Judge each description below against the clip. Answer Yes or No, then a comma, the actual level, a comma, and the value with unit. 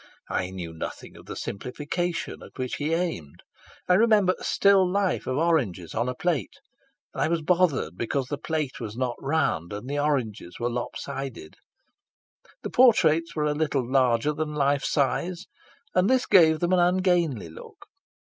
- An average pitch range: No, wide, 5.9 semitones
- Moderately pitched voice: Yes, medium, 150 Hz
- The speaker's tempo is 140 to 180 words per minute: Yes, average, 170 wpm